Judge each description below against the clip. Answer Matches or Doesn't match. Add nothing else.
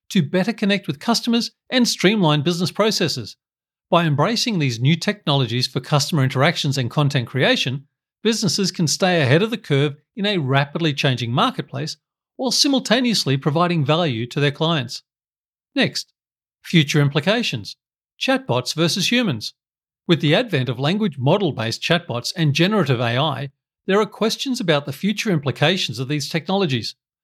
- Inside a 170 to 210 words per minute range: Doesn't match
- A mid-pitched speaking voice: Matches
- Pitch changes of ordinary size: Doesn't match